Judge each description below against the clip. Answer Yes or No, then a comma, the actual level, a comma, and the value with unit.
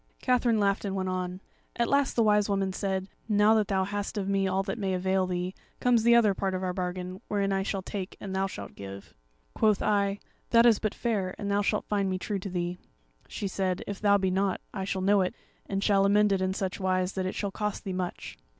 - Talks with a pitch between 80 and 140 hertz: No, high, 195 Hz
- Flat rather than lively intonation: Yes, narrow, 1.7 semitones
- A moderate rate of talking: No, fast, 240 wpm